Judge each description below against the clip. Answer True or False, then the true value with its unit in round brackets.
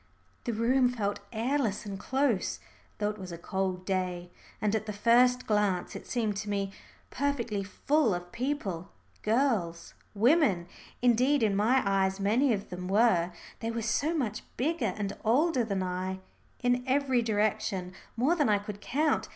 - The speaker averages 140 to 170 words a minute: True (160 wpm)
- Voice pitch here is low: False (215 Hz)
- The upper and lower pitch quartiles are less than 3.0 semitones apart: False (4.4 semitones)